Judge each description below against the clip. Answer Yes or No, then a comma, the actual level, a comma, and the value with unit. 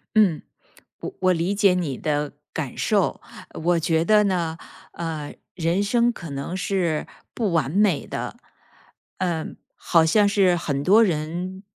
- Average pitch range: Yes, average, 3.6 semitones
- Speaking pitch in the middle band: Yes, medium, 175 Hz